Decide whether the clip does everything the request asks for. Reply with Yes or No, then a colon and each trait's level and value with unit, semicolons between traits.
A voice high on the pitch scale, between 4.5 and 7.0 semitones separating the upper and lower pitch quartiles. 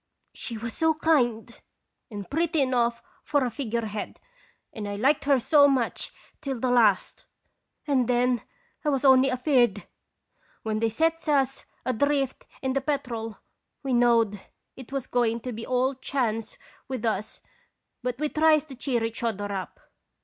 No: very high, 250 Hz; average, 3.5 semitones